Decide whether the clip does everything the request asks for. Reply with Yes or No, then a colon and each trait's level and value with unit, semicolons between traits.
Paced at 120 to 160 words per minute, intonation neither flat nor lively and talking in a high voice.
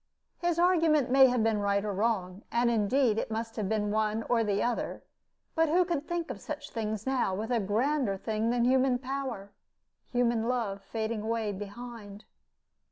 No: average, 175 wpm; average, 3.6 semitones; high, 230 Hz